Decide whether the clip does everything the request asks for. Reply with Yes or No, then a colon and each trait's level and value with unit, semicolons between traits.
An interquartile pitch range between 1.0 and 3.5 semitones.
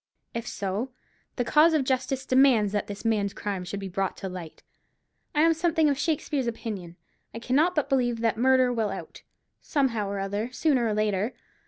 No: average, 4.9 semitones